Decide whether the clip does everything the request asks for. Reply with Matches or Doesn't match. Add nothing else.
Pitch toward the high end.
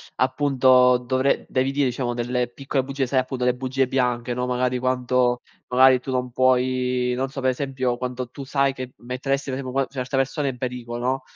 Doesn't match